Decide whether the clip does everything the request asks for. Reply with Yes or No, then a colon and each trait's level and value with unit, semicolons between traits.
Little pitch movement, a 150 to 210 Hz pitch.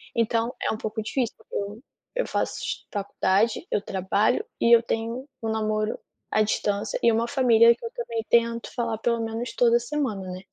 No: narrow, 1.7 semitones; high, 225 Hz